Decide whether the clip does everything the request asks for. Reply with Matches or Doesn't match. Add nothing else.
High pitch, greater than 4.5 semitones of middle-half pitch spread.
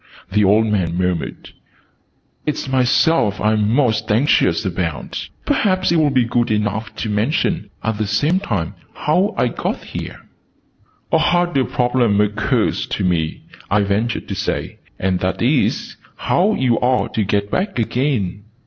Doesn't match